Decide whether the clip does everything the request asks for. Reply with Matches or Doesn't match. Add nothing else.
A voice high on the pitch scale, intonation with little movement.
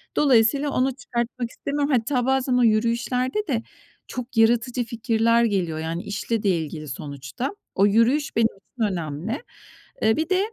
Doesn't match